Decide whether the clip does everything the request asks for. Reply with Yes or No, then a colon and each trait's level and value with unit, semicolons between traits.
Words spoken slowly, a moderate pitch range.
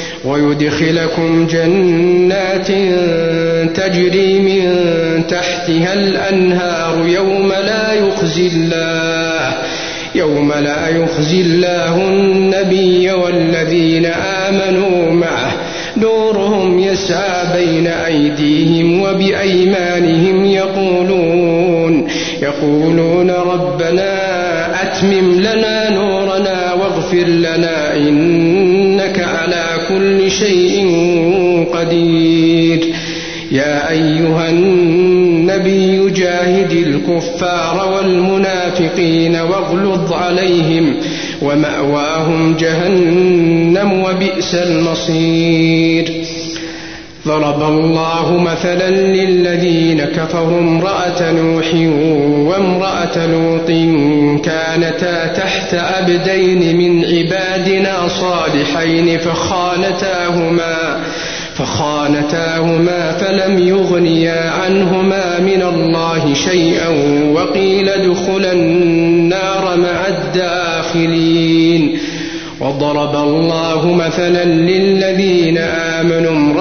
No: slow, 60 wpm; narrow, 2.1 semitones